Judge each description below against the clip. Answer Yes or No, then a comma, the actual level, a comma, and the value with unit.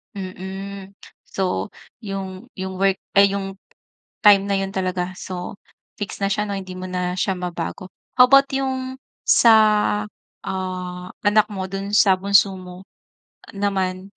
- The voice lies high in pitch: Yes, high, 195 Hz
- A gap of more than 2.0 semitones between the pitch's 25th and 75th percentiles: No, narrow, 1.3 semitones